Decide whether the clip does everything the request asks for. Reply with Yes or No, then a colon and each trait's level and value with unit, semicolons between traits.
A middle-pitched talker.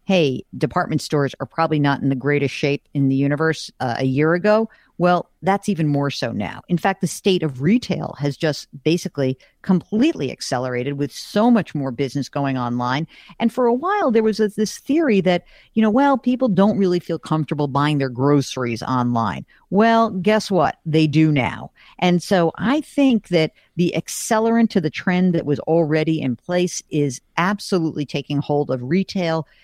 Yes: medium, 160 Hz